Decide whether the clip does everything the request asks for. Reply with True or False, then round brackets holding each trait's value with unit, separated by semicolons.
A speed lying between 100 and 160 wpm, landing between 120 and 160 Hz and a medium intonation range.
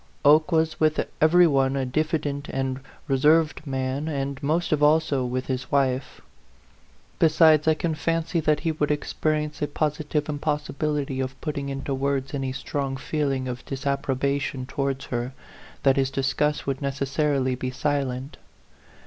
False (150 wpm; 140 Hz; 2.3 semitones)